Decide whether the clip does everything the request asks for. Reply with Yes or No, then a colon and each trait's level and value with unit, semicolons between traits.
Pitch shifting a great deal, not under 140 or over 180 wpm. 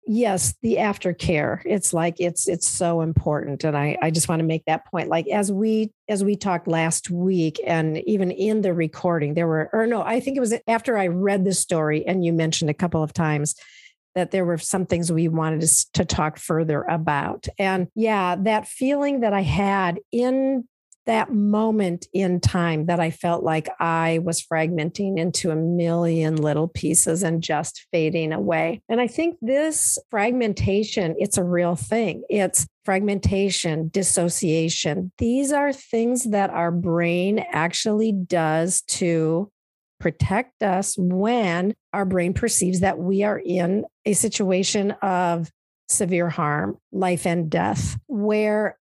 No: average, 4.1 semitones; average, 160 wpm